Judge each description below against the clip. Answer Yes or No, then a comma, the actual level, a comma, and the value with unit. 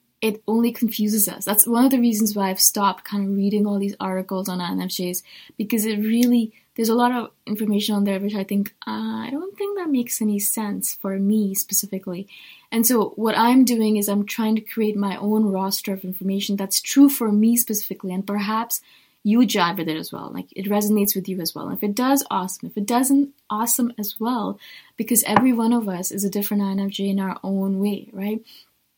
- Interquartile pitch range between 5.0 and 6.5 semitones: No, average, 2.8 semitones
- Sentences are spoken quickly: Yes, fast, 215 wpm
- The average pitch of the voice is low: No, high, 210 Hz